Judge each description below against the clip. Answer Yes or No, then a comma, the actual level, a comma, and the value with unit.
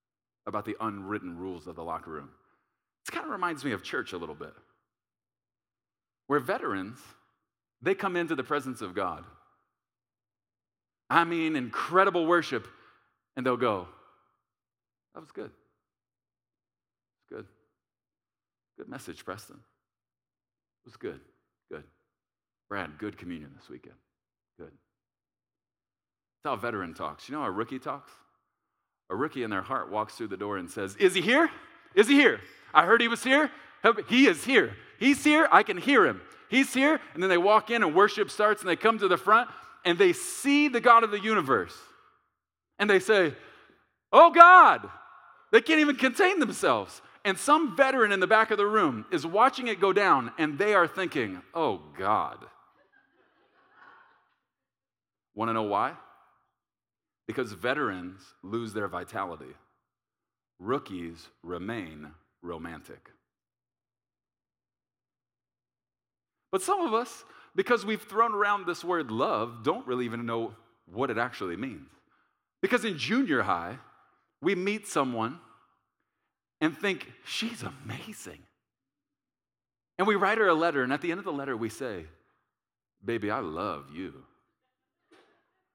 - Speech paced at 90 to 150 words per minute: Yes, average, 145 wpm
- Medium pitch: Yes, medium, 165 Hz